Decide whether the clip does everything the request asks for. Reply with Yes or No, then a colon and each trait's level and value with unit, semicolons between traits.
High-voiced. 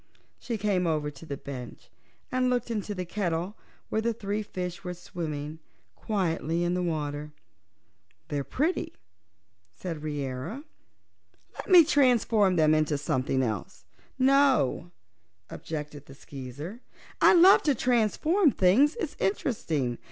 No: medium, 180 Hz